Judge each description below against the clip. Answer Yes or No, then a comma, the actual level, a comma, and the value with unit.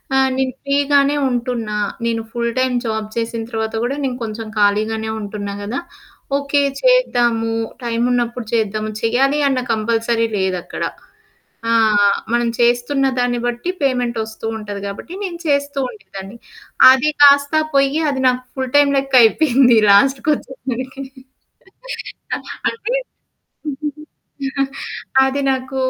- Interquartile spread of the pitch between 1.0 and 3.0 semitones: No, average, 3.4 semitones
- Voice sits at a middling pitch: No, high, 245 Hz